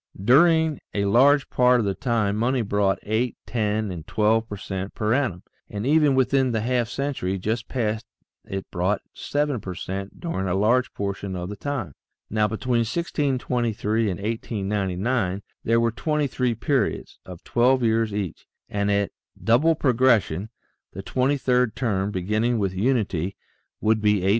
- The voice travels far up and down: No, average, 4.1 semitones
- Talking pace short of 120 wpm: No, average, 155 wpm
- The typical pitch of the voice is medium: No, low, 110 Hz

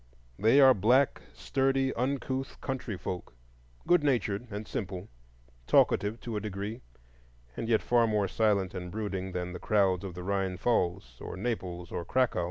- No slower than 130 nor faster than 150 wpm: No, average, 160 wpm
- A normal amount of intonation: Yes, average, 4.8 semitones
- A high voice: No, low, 105 Hz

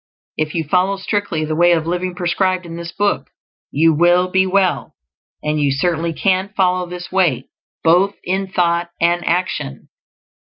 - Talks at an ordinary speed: Yes, average, 160 wpm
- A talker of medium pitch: Yes, medium, 175 Hz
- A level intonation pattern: Yes, narrow, 2.2 semitones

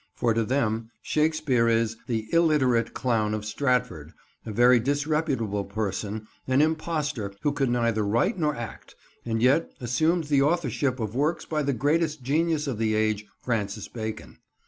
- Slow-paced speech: No, average, 155 wpm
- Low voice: Yes, low, 125 Hz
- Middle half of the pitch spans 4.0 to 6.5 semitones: Yes, average, 5.3 semitones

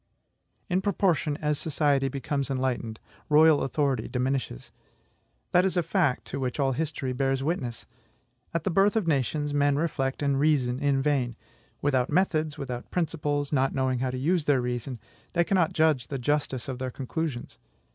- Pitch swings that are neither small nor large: Yes, average, 3.2 semitones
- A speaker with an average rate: Yes, average, 165 wpm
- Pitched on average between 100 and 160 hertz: Yes, medium, 140 Hz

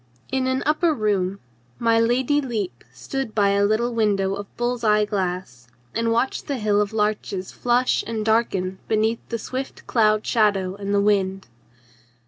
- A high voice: Yes, high, 215 Hz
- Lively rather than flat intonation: No, average, 3.1 semitones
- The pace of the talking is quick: No, average, 160 wpm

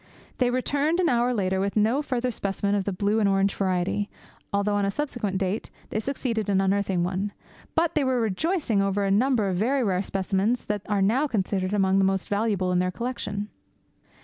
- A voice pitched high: Yes, high, 205 Hz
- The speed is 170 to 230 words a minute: Yes, average, 200 wpm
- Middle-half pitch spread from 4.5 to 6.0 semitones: No, average, 3.9 semitones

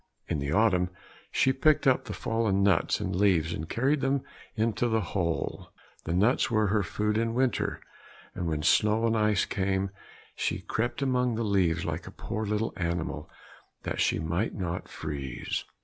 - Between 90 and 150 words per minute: No, average, 170 wpm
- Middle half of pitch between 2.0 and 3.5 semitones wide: No, average, 4.6 semitones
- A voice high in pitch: No, low, 105 Hz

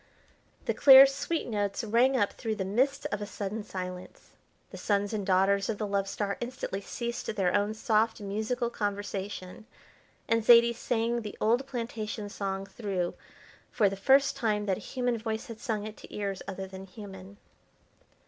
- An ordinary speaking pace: Yes, average, 170 wpm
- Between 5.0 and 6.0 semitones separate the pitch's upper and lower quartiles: No, average, 3.0 semitones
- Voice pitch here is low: No, high, 210 Hz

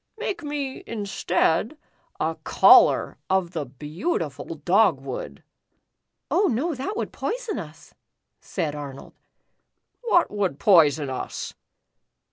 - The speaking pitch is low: No, high, 190 Hz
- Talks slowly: Yes, slow, 105 wpm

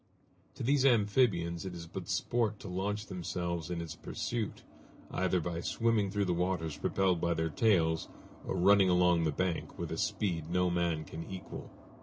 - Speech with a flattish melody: No, average, 3.2 semitones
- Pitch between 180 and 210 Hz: No, very low, 90 Hz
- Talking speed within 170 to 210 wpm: Yes, average, 175 wpm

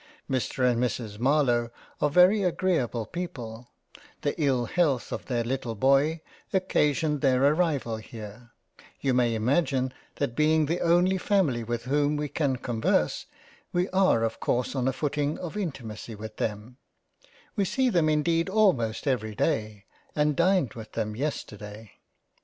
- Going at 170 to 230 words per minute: No, average, 145 wpm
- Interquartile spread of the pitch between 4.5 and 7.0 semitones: Yes, wide, 5.6 semitones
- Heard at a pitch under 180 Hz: Yes, low, 135 Hz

